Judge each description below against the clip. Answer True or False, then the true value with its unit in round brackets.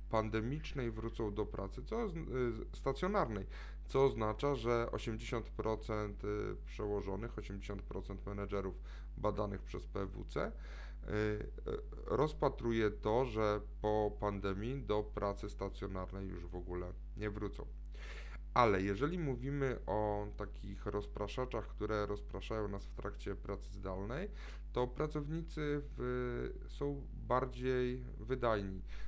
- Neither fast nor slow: False (100 wpm)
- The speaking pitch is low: True (105 Hz)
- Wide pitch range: False (4.1 semitones)